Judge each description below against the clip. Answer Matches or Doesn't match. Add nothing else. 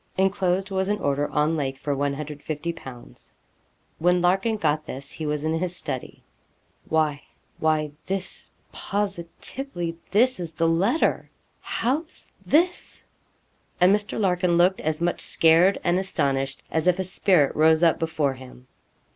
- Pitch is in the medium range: Matches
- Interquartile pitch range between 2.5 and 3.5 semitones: Doesn't match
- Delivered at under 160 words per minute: Matches